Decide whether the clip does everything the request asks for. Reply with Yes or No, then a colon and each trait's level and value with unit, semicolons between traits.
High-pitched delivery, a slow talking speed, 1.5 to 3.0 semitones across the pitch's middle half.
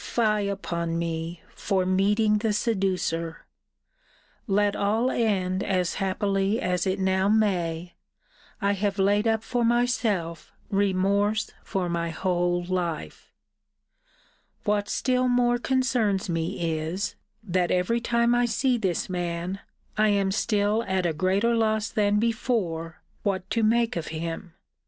No: high, 195 Hz; slow, 130 wpm; average, 3.5 semitones